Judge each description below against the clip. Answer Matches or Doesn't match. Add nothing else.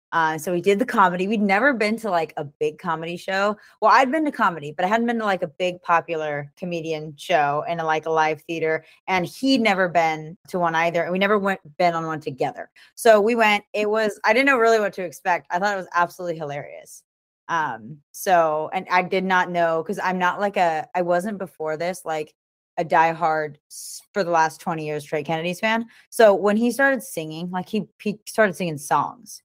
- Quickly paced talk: Matches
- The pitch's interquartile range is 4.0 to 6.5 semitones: Matches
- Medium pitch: Matches